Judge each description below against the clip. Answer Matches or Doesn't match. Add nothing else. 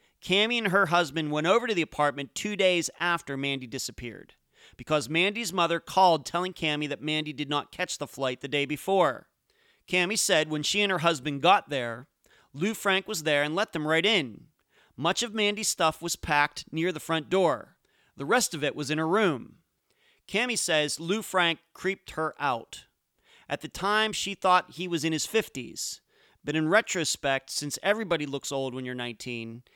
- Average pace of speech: Matches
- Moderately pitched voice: Matches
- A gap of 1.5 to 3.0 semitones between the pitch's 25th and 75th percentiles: Doesn't match